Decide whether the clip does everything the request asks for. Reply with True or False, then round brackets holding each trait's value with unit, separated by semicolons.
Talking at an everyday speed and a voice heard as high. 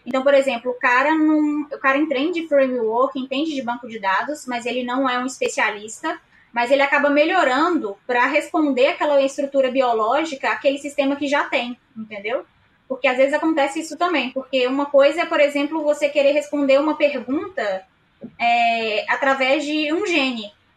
True (170 wpm; 275 Hz)